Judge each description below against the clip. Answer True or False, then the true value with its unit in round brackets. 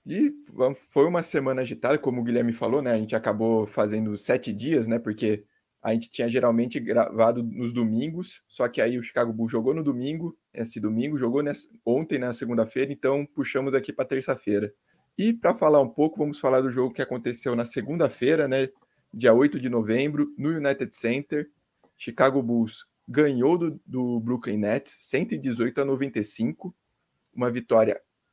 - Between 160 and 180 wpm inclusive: True (170 wpm)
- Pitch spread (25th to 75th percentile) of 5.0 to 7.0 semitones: False (3.6 semitones)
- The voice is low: True (130 Hz)